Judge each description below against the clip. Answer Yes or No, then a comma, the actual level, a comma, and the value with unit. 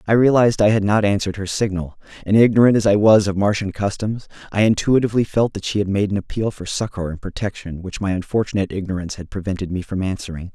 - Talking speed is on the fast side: Yes, fast, 215 wpm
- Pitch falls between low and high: No, low, 100 Hz